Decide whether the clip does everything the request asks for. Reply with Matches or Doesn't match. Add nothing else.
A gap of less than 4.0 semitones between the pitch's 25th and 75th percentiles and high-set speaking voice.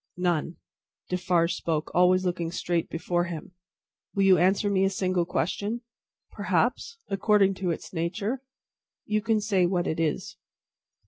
Doesn't match